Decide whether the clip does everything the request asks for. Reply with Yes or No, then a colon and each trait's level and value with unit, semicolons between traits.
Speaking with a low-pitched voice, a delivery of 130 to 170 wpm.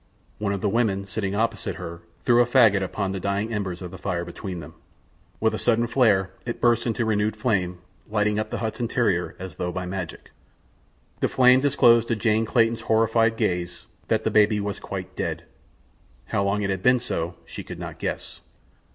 No: low, 105 Hz; average, 195 wpm